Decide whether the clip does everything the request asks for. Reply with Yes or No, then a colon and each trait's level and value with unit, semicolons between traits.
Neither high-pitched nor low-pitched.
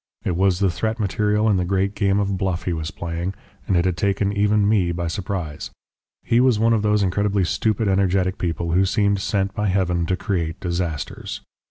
No: very low, 95 Hz